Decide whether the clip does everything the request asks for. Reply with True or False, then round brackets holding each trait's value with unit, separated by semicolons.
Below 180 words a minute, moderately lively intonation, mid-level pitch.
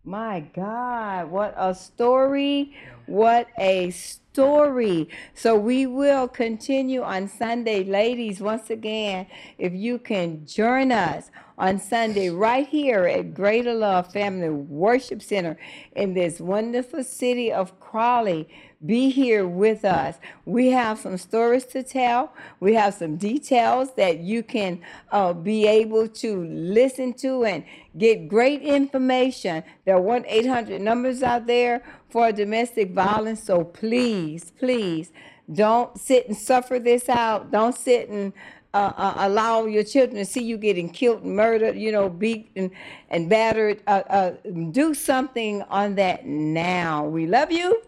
False (140 wpm; 4.2 semitones; 220 Hz)